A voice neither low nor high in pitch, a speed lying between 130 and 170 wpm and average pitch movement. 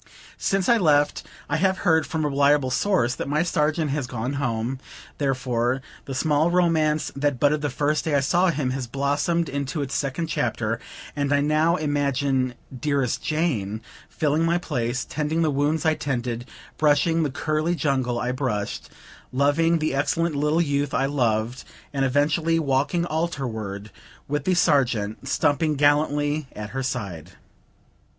Yes: medium, 145 Hz; average, 155 wpm; average, 3.4 semitones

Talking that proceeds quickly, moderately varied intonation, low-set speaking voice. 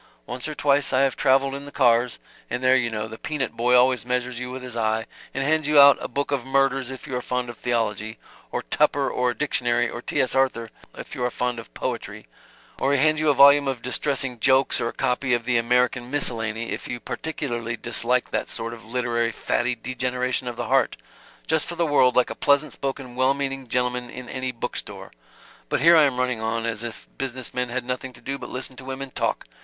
No: fast, 230 wpm; narrow, 2.3 semitones; low, 125 Hz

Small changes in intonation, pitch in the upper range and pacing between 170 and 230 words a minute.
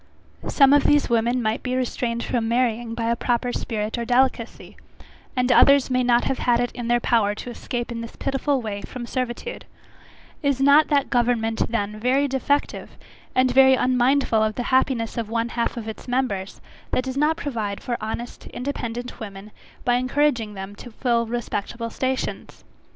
Yes: narrow, 2.2 semitones; high, 245 Hz; average, 175 wpm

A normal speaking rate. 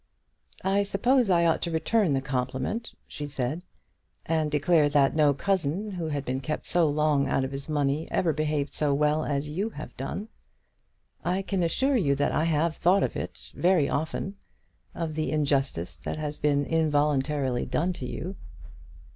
Yes: average, 175 wpm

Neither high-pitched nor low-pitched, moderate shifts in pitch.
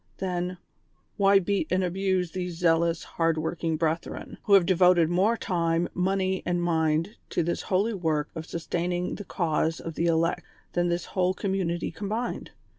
No: medium, 175 Hz; narrow, 2.2 semitones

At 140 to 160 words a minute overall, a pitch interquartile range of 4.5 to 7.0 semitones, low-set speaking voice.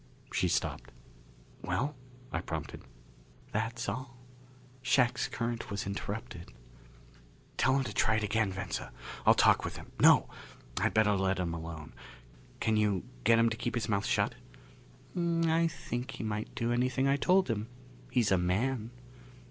No: average, 150 wpm; average, 4.1 semitones; low, 115 Hz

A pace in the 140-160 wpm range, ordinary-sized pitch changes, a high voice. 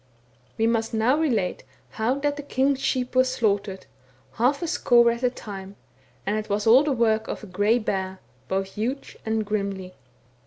No: average, 180 wpm; average, 4.0 semitones; high, 225 Hz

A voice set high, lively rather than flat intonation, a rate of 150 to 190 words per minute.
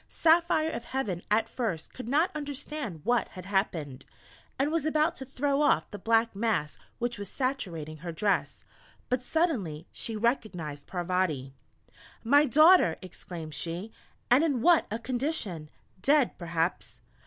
No: high, 225 Hz; wide, 8.3 semitones; average, 140 wpm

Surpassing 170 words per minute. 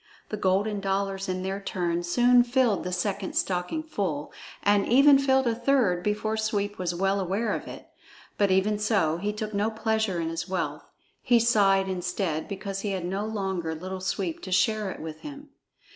Yes: average, 185 wpm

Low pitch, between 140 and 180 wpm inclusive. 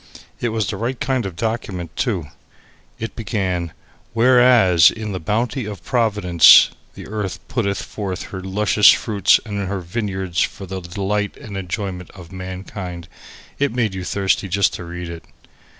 Yes: low, 100 Hz; average, 160 wpm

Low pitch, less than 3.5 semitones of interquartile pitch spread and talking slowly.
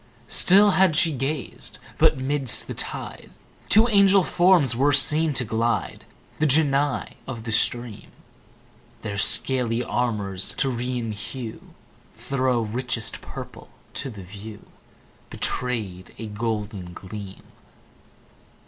No: low, 125 Hz; average, 4.9 semitones; slow, 110 wpm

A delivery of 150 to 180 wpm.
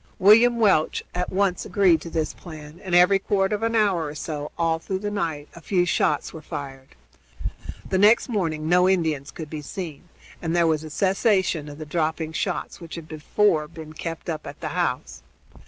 No: average, 195 wpm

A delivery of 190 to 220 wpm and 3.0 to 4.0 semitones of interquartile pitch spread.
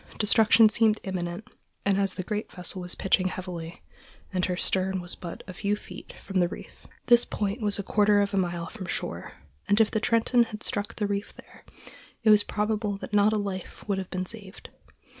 No: average, 200 wpm; narrow, 2.4 semitones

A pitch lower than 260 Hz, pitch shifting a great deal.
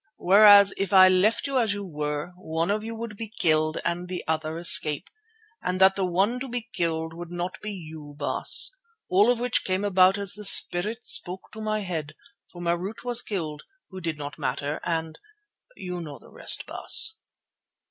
No: medium, 185 Hz; average, 4.5 semitones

